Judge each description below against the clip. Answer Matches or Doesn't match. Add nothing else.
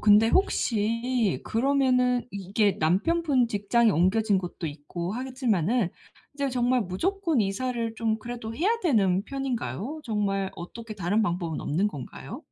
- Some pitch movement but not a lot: Matches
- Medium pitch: Doesn't match